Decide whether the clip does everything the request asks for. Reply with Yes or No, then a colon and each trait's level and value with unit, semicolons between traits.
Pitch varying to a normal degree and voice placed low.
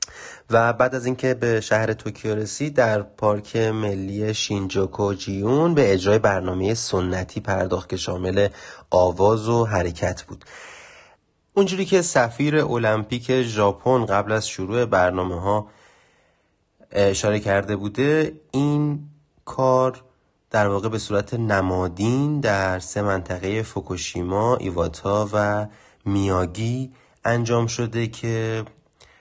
Yes: average, 3.9 semitones; low, 105 Hz